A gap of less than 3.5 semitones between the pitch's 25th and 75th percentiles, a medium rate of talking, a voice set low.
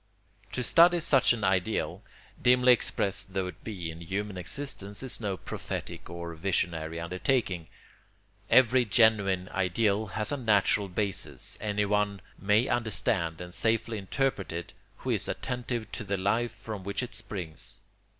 No: average, 3.9 semitones; average, 145 wpm; low, 105 Hz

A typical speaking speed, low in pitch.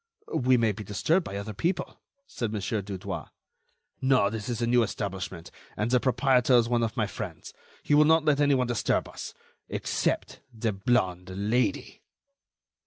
Yes: average, 160 wpm; low, 115 Hz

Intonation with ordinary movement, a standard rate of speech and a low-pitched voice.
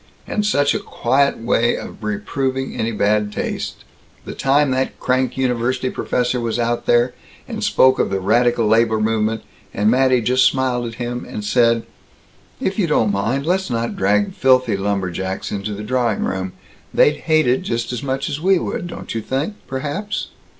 Yes: average, 3.4 semitones; average, 175 wpm; low, 120 Hz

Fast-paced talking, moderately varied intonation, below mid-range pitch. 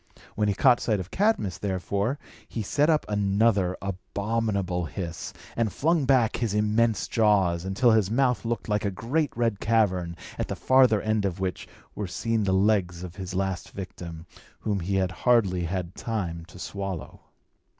No: average, 170 wpm; average, 3.6 semitones; low, 100 Hz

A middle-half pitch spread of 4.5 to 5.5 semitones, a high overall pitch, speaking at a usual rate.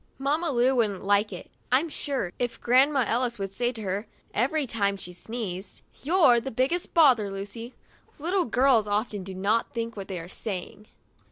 Yes: average, 5.0 semitones; high, 230 Hz; average, 175 wpm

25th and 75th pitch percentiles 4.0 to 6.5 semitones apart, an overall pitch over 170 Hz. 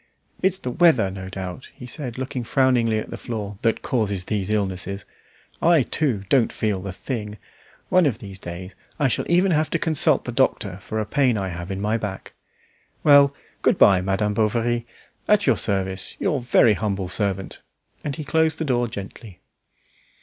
No: wide, 5.6 semitones; low, 110 Hz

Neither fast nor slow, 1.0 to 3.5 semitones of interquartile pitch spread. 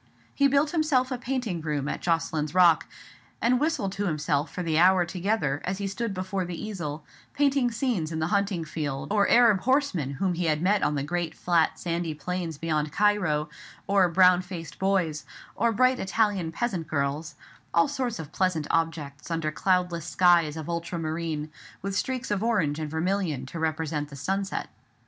No: average, 175 wpm; average, 4.3 semitones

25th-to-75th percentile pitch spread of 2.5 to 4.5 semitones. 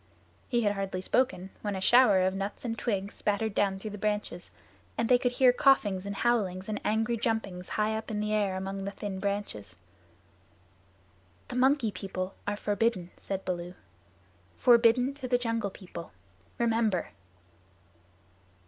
Yes: average, 3.3 semitones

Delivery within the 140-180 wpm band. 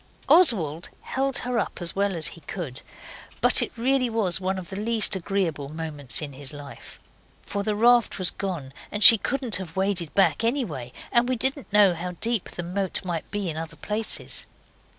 No: average, 190 wpm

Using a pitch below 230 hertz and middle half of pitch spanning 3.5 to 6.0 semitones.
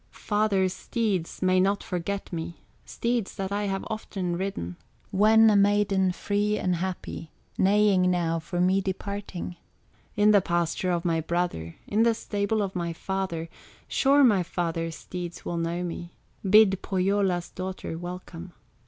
No: medium, 185 Hz; average, 2.8 semitones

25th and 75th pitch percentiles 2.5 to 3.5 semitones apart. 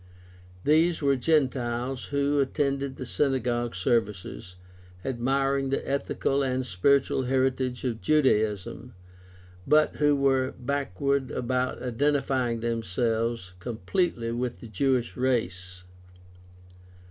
Yes: average, 2.9 semitones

